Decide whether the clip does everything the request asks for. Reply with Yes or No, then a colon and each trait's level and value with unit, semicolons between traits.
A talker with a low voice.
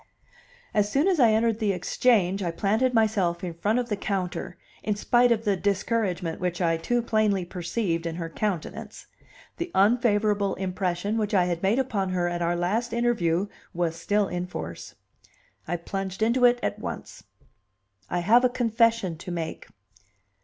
No: high, 200 Hz